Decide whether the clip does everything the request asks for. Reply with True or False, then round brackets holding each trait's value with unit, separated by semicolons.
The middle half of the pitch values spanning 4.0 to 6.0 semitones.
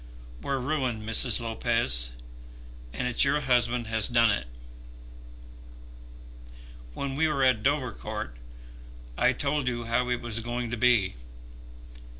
False (2.6 semitones)